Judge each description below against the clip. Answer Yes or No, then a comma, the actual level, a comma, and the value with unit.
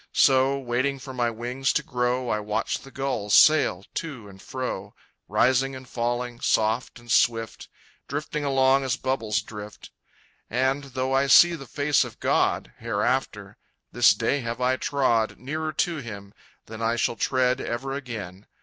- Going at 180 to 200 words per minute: No, average, 160 wpm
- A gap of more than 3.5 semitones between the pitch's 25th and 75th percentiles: No, average, 2.7 semitones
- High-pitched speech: No, low, 125 Hz